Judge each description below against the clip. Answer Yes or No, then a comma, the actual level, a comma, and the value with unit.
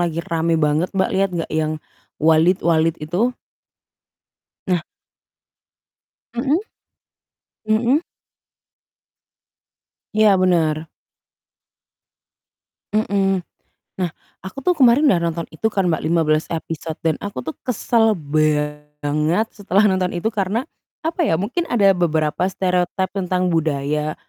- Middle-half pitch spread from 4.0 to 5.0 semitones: Yes, average, 4.3 semitones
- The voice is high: No, medium, 175 Hz